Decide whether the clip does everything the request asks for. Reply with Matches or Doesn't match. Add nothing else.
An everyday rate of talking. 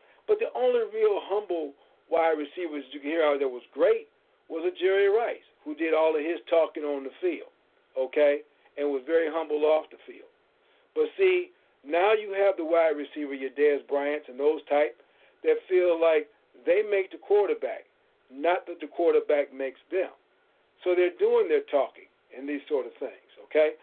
Matches